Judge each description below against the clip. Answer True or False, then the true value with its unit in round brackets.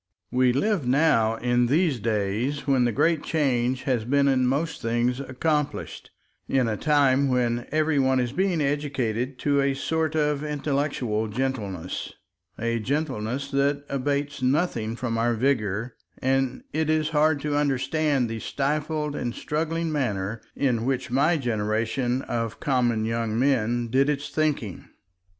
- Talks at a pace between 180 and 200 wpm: False (145 wpm)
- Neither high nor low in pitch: False (130 Hz)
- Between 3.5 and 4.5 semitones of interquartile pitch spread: True (3.8 semitones)